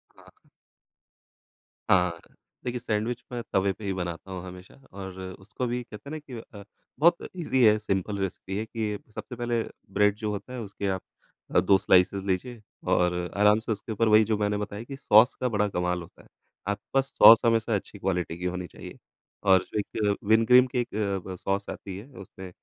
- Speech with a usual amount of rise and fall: Yes, average, 3.3 semitones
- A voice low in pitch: Yes, low, 105 Hz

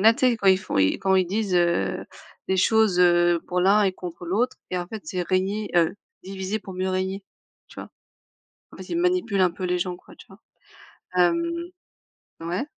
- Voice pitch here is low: No, medium, 185 Hz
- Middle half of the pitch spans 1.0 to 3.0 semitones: Yes, narrow, 2.6 semitones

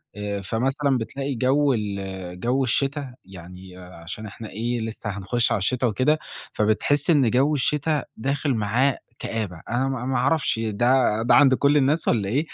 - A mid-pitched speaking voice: No, low, 120 Hz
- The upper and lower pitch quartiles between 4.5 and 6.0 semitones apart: Yes, average, 4.9 semitones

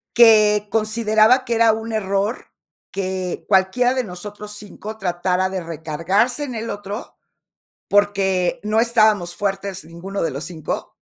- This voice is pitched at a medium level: No, high, 205 Hz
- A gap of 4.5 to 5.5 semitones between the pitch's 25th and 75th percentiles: No, average, 2.8 semitones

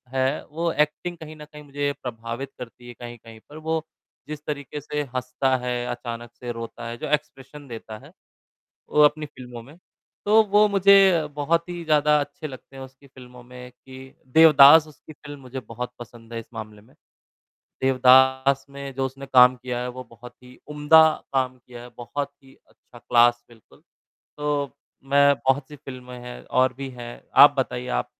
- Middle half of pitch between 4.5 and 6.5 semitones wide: No, average, 3.3 semitones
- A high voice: No, low, 130 Hz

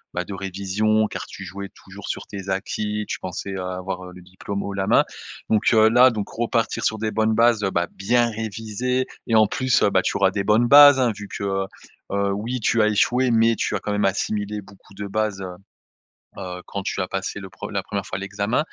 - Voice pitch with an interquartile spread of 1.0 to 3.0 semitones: Yes, narrow, 2.4 semitones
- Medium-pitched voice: No, low, 105 Hz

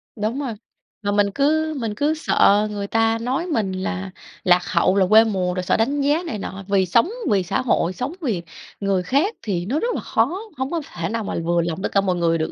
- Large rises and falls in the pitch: Yes, wide, 6.1 semitones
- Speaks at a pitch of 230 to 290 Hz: No, high, 210 Hz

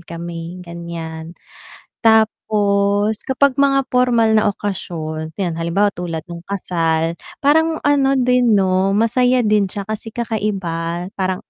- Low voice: No, high, 200 Hz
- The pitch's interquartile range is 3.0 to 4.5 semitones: No, average, 5.2 semitones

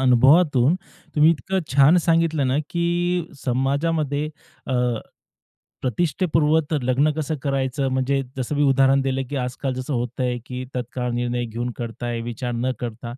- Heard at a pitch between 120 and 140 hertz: Yes, low, 135 Hz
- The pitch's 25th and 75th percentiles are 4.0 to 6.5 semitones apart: No, average, 3.5 semitones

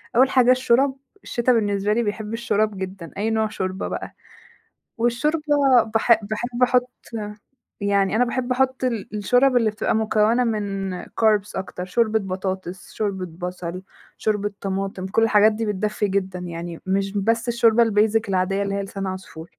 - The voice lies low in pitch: No, high, 210 Hz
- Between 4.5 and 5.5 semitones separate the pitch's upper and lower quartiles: No, average, 3.2 semitones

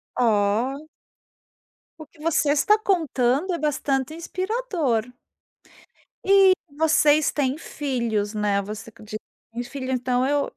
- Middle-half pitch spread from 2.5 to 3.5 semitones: No, average, 5.1 semitones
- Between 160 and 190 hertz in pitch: No, very high, 275 Hz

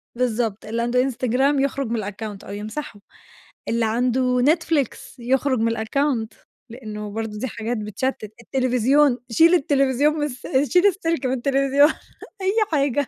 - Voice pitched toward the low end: No, very high, 255 Hz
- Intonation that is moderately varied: Yes, average, 3.8 semitones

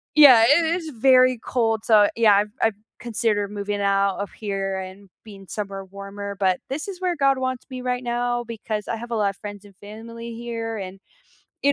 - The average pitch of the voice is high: Yes, high, 220 Hz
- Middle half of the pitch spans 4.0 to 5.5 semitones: No, average, 3.4 semitones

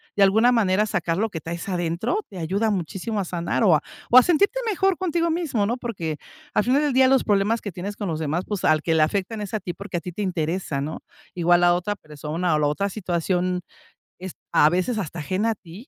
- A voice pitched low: No, high, 190 Hz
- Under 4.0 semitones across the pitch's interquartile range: No, average, 4.7 semitones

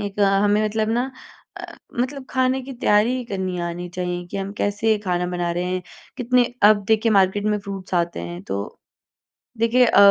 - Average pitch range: Yes, average, 4.3 semitones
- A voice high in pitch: Yes, high, 205 Hz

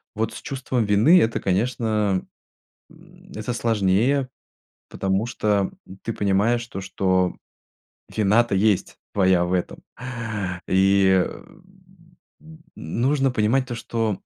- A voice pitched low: Yes, low, 110 Hz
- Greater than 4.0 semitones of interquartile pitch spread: Yes, average, 4.4 semitones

